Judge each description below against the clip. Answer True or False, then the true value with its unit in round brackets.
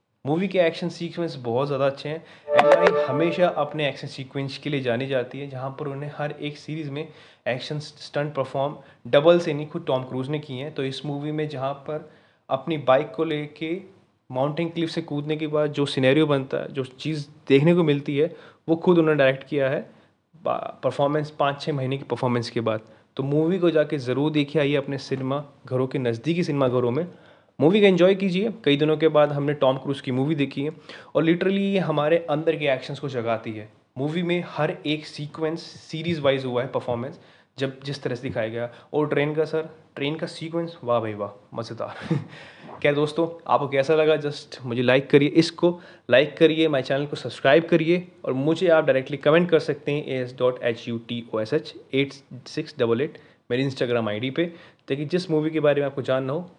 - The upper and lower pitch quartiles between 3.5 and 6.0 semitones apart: False (3.0 semitones)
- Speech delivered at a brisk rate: True (210 wpm)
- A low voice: False (145 Hz)